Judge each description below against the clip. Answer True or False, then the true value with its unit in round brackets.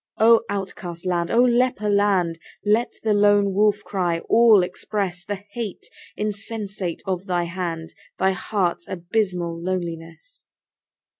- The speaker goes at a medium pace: False (125 wpm)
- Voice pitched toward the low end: False (195 Hz)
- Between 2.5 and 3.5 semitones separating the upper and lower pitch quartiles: True (3.2 semitones)